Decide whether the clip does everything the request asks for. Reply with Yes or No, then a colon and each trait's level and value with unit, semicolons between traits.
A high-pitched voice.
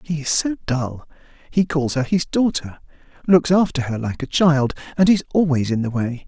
No: medium, 150 Hz